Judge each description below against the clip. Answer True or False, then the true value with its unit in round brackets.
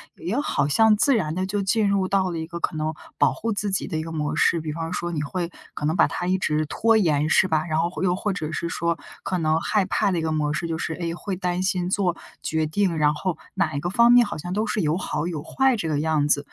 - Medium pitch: True (170 Hz)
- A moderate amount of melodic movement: True (3.6 semitones)